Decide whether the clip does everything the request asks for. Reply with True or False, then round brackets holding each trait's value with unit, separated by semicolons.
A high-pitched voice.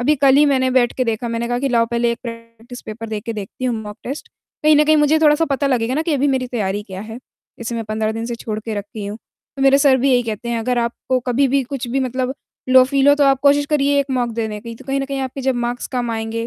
True (245 Hz)